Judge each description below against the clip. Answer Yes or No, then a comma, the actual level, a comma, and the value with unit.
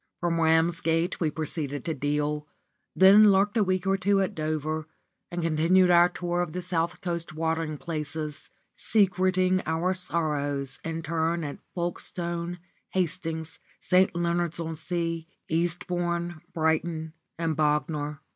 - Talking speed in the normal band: No, slow, 130 wpm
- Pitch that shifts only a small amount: Yes, narrow, 2.0 semitones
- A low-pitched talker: No, medium, 165 Hz